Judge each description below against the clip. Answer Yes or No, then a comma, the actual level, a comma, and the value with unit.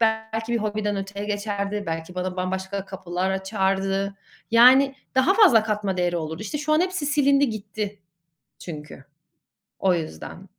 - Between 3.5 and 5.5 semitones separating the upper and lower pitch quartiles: No, average, 3.0 semitones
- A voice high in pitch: Yes, high, 200 Hz